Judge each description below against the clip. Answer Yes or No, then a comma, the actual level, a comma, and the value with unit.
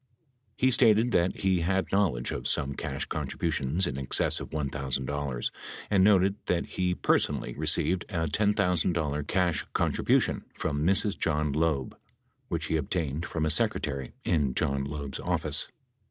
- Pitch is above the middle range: No, very low, 80 Hz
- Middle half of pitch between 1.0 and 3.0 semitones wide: No, average, 4.8 semitones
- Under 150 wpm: Yes, average, 140 wpm